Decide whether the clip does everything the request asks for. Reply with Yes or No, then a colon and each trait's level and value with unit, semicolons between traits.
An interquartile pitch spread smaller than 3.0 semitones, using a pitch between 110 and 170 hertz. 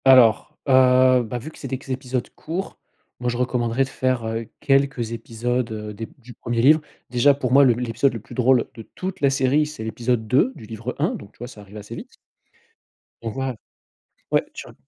Yes: narrow, 2.6 semitones; low, 125 Hz